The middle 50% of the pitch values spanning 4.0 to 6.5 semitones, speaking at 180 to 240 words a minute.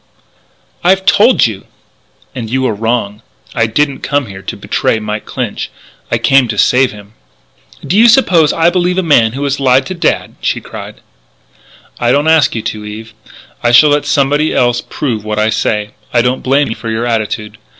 Yes: average, 4.9 semitones; average, 190 wpm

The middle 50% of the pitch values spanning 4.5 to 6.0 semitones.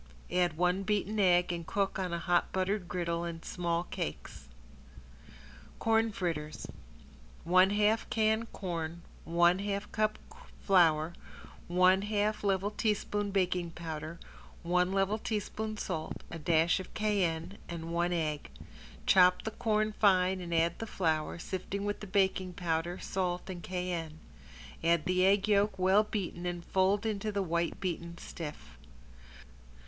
No: average, 3.0 semitones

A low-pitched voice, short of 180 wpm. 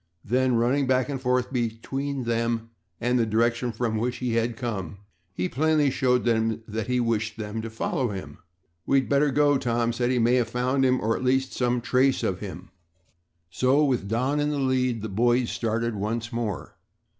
No: low, 120 Hz; average, 190 wpm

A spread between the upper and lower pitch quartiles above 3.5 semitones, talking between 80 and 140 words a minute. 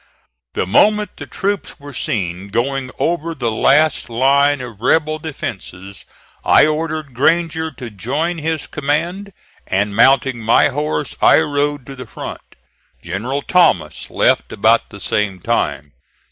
Yes: wide, 5.6 semitones; slow, 135 wpm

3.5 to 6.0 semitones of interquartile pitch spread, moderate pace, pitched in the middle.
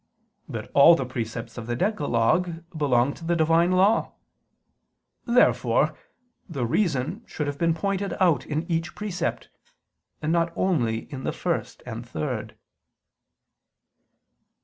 No: wide, 5.5 semitones; slow, 125 wpm; medium, 160 Hz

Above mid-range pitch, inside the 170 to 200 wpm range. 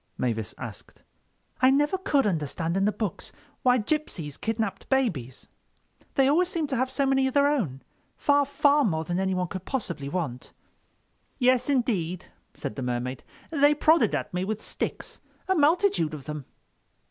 No: high, 225 Hz; average, 155 wpm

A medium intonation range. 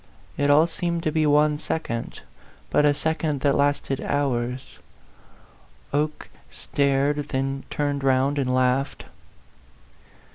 No: narrow, 1.7 semitones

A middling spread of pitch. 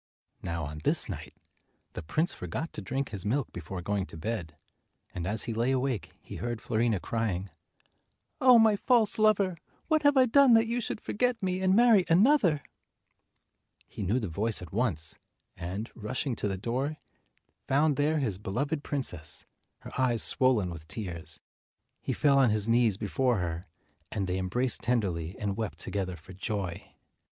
No: wide, 8.3 semitones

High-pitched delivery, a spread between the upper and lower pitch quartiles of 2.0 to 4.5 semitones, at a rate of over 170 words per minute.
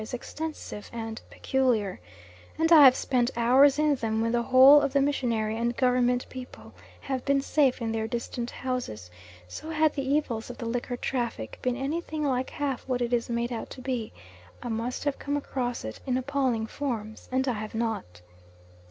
Yes: very high, 250 Hz; average, 2.9 semitones; average, 185 wpm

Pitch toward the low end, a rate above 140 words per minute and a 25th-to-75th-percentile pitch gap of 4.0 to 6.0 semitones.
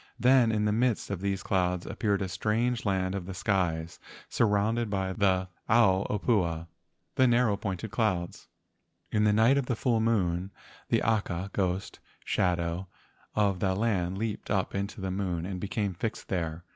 No: low, 100 Hz; average, 170 wpm; average, 3.1 semitones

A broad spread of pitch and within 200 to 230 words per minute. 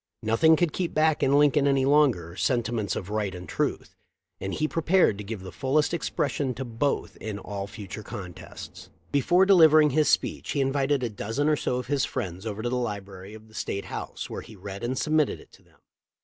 Yes: wide, 6.3 semitones; fast, 205 wpm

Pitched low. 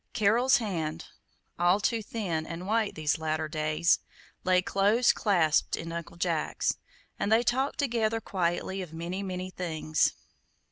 No: medium, 185 Hz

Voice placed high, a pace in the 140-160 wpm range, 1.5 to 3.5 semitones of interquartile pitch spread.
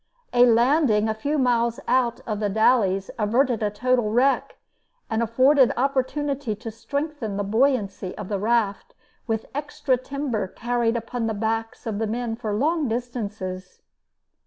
Yes: high, 230 Hz; average, 150 wpm; average, 3.2 semitones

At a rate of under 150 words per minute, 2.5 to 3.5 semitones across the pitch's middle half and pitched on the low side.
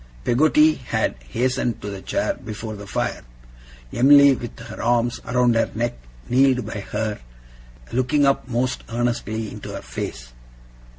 Yes: average, 140 wpm; average, 2.8 semitones; low, 120 Hz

